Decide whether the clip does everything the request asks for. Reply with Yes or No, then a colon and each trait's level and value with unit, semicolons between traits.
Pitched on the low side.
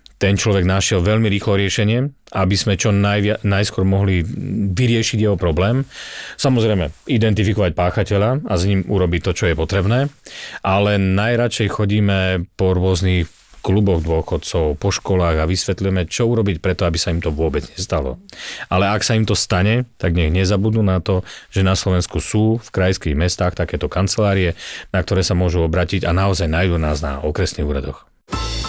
Yes: very low, 95 Hz